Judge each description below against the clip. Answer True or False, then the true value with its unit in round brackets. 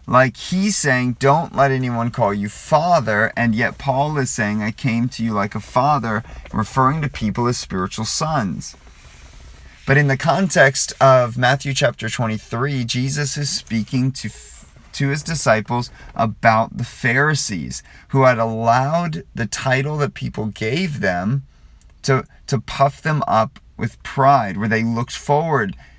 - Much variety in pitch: False (4.0 semitones)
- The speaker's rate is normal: True (150 wpm)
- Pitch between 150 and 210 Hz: False (125 Hz)